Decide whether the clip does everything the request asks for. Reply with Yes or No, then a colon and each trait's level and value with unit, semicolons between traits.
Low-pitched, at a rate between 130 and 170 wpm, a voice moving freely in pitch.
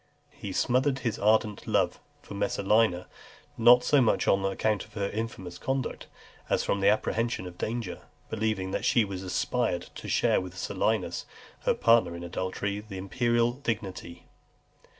No: low, 105 Hz; average, 145 wpm; average, 3.7 semitones